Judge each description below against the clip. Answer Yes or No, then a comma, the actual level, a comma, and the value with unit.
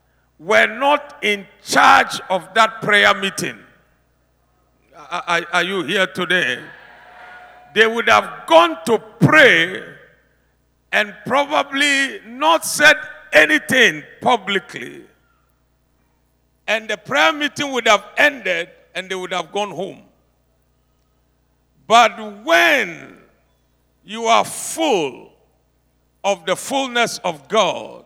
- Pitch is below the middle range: No, high, 190 Hz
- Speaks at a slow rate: Yes, slow, 105 wpm